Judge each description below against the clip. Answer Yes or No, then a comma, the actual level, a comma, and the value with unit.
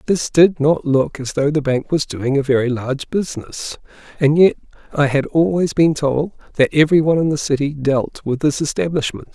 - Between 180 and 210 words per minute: Yes, average, 200 wpm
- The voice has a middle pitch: Yes, medium, 145 Hz